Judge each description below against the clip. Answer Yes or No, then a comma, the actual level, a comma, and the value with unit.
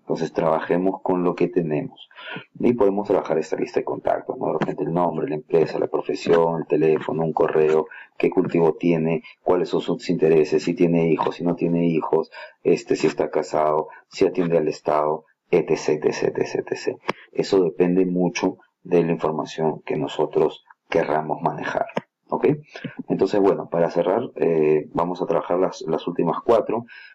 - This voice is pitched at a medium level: No, very low, 85 Hz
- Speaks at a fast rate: No, average, 165 wpm